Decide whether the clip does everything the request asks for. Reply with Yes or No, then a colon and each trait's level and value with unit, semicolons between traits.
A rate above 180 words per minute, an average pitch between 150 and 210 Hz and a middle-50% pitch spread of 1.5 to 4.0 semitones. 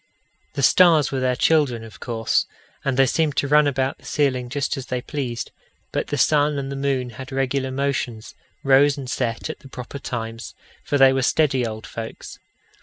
No: average, 190 wpm; low, 135 Hz; narrow, 2.4 semitones